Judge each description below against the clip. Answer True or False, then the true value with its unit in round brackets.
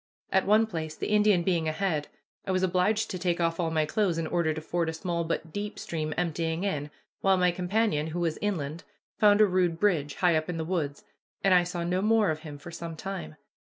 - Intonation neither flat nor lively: True (3.1 semitones)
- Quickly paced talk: True (225 wpm)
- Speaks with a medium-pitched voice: True (175 Hz)